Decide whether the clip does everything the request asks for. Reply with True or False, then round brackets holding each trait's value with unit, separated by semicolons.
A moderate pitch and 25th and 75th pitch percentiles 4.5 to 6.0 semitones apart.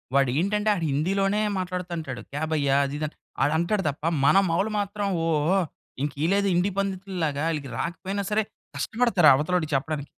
True (175 Hz; 4.9 semitones)